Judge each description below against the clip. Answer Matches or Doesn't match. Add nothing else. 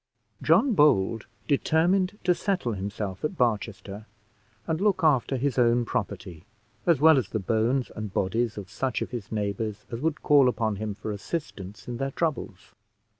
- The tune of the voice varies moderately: Doesn't match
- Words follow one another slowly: Doesn't match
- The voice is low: Matches